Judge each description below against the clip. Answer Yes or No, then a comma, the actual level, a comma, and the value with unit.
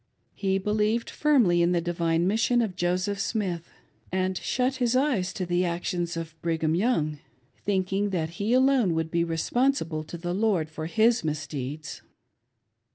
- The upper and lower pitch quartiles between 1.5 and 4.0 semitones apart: No, average, 4.7 semitones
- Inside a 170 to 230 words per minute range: No, average, 155 wpm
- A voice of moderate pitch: Yes, medium, 180 Hz